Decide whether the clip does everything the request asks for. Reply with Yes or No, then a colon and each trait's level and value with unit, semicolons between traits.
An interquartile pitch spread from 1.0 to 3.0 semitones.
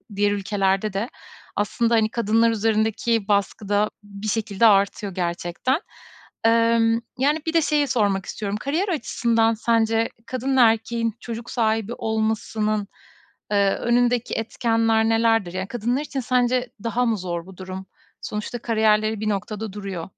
Yes: narrow, 2.4 semitones